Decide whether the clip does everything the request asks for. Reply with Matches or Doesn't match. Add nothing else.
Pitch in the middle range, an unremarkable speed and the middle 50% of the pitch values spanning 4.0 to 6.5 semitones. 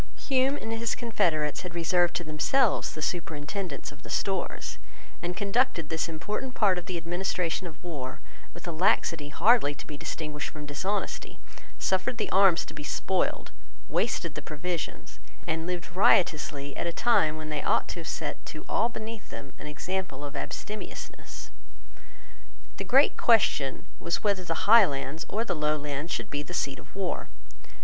Matches